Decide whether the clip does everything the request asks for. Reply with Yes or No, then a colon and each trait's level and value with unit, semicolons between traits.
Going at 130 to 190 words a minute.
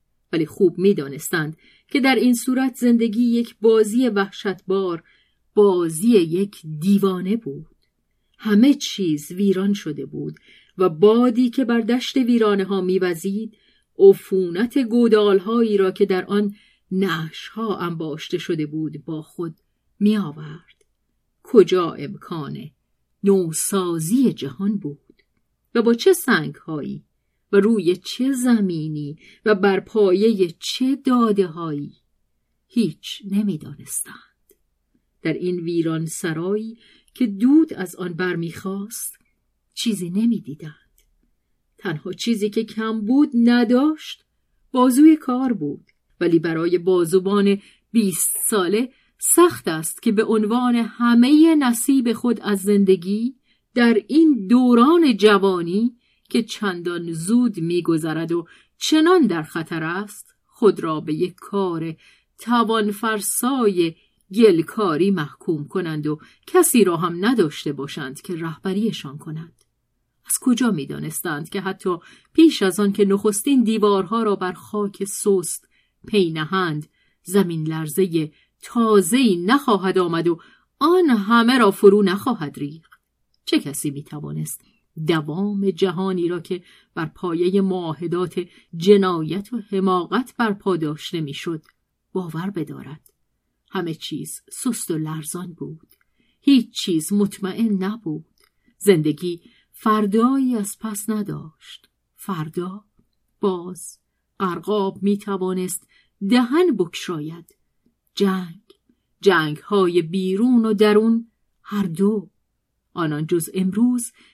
No: average, 110 wpm